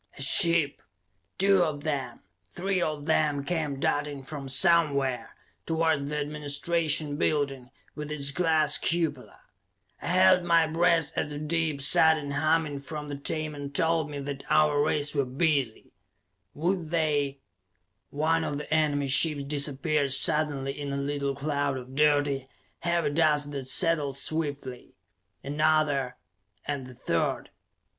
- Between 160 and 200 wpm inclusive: No, slow, 135 wpm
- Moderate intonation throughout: No, narrow, 2.2 semitones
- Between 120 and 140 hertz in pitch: No, medium, 150 Hz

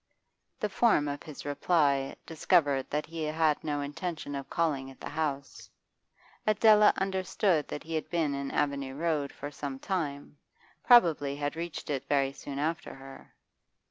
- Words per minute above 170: No, average, 155 wpm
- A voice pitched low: No, medium, 150 Hz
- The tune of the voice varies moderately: Yes, average, 3.1 semitones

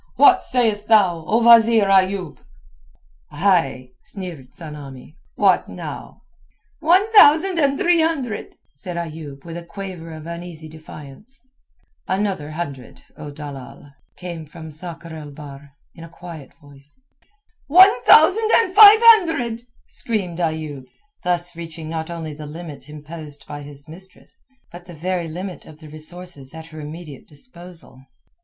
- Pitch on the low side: No, medium, 170 Hz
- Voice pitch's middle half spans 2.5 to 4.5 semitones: No, average, 5.2 semitones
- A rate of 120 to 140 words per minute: Yes, slow, 135 wpm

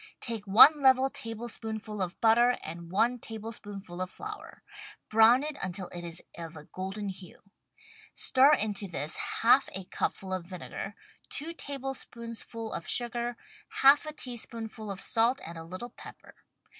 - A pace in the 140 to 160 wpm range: Yes, average, 150 wpm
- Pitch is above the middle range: Yes, high, 220 Hz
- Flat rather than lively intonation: No, average, 4.6 semitones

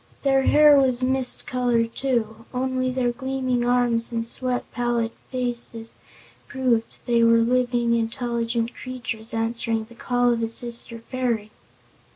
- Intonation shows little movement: Yes, narrow, 1.7 semitones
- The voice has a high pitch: Yes, high, 240 Hz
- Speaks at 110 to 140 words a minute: Yes, slow, 135 wpm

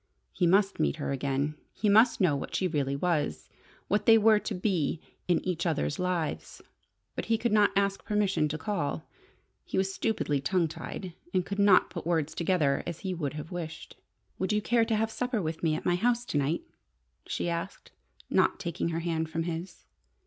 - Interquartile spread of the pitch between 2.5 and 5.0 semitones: Yes, average, 4.3 semitones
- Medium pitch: Yes, medium, 175 Hz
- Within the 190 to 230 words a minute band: Yes, average, 195 wpm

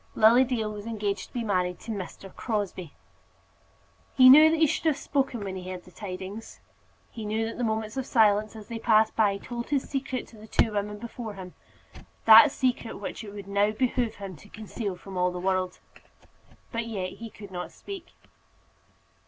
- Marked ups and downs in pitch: No, average, 3.0 semitones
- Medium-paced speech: Yes, average, 195 wpm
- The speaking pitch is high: Yes, high, 215 Hz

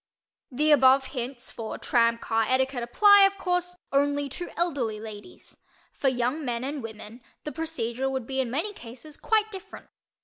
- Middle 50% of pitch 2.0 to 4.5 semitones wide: No, average, 5.1 semitones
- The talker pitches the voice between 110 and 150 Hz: No, very high, 265 Hz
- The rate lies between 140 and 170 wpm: Yes, average, 165 wpm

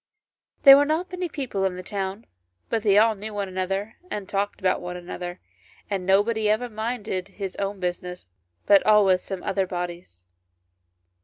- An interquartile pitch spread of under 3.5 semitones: Yes, average, 2.8 semitones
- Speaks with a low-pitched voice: No, high, 195 Hz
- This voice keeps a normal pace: Yes, average, 165 wpm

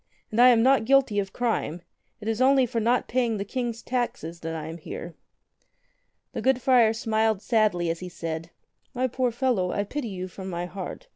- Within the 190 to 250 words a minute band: Yes, average, 195 wpm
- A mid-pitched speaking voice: No, high, 220 Hz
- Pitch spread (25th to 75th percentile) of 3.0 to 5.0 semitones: No, wide, 5.4 semitones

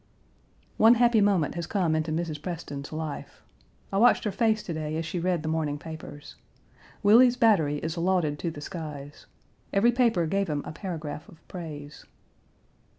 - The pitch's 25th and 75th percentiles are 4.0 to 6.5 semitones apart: Yes, average, 4.5 semitones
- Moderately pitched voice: Yes, medium, 165 Hz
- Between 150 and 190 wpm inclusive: Yes, average, 165 wpm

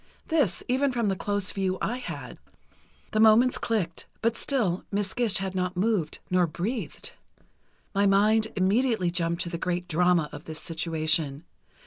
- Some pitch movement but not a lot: Yes, average, 4.4 semitones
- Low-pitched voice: No, high, 190 Hz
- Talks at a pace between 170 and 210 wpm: No, average, 155 wpm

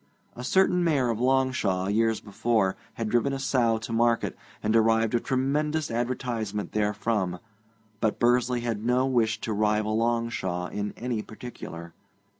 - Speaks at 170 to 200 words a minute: No, average, 145 wpm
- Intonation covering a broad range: No, average, 2.7 semitones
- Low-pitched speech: Yes, low, 115 Hz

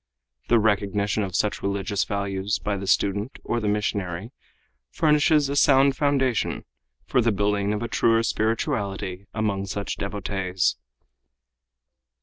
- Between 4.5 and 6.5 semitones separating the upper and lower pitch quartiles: No, average, 2.9 semitones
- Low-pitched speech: Yes, low, 105 Hz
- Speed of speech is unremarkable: No, slow, 130 wpm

